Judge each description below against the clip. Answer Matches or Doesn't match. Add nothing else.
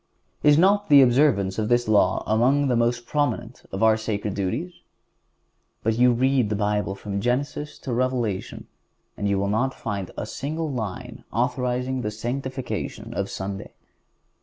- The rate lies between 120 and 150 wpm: Doesn't match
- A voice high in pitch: Doesn't match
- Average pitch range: Matches